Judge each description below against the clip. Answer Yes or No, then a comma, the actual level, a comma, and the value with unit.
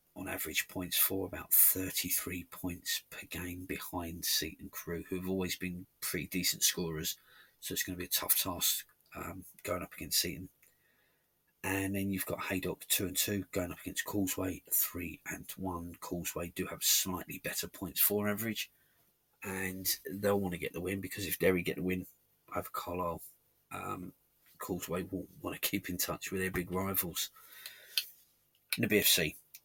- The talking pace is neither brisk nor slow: Yes, average, 170 wpm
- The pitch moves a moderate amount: No, narrow, 1.5 semitones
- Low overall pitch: Yes, very low, 95 Hz